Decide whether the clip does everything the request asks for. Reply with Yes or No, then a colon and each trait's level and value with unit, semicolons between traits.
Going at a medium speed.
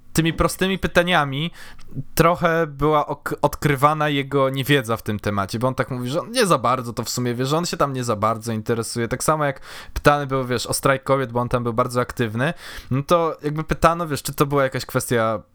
No: fast, 225 wpm